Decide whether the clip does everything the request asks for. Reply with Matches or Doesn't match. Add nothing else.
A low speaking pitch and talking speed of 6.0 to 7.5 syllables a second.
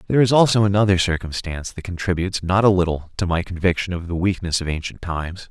Matches